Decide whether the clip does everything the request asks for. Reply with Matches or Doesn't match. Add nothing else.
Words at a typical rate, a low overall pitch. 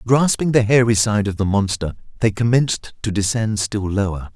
Matches